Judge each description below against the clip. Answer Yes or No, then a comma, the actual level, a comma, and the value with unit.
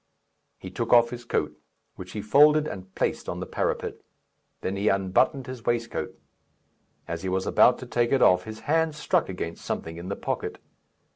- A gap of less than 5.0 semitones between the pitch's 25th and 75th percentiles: No, average, 5.3 semitones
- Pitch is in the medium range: No, low, 110 Hz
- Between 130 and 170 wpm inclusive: No, average, 185 wpm